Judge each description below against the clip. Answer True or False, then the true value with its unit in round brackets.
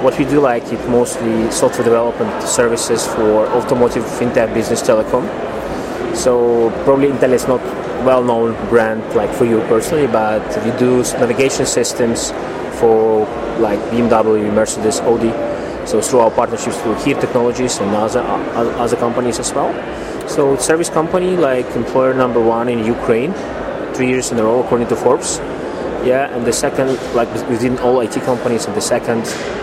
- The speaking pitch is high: False (120 Hz)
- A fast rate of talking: False (155 wpm)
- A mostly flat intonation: True (2.0 semitones)